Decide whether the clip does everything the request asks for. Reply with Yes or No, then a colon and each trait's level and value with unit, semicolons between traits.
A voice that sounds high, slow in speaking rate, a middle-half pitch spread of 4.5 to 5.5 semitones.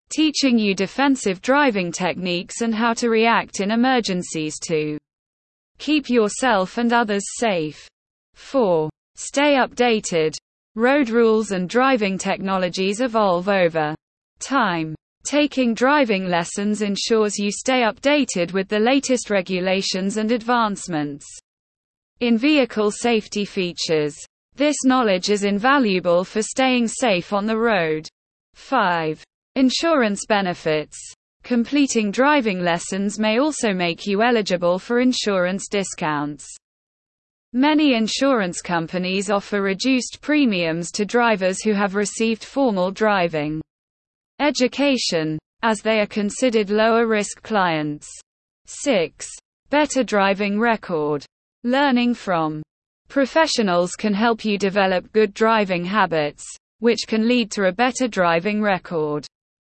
Yes: high, 210 Hz; slow, 115 wpm; average, 5.2 semitones